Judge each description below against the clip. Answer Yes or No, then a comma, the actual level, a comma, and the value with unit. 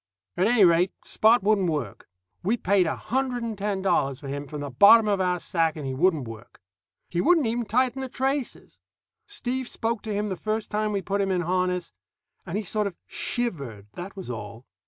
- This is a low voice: No, high, 195 Hz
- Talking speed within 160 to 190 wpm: No, fast, 205 wpm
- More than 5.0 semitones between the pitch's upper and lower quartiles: Yes, wide, 5.5 semitones